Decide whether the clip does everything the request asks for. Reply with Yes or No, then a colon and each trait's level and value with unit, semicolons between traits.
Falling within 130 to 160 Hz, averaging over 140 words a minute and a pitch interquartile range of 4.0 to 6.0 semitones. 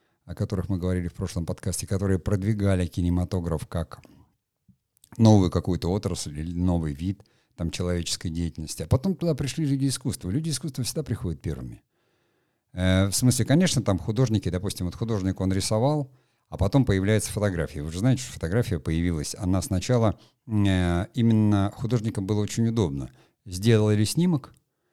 No: low, 100 Hz; average, 150 wpm; average, 4.7 semitones